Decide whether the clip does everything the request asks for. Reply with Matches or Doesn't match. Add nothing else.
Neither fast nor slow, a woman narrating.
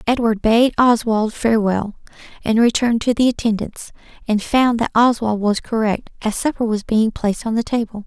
Matches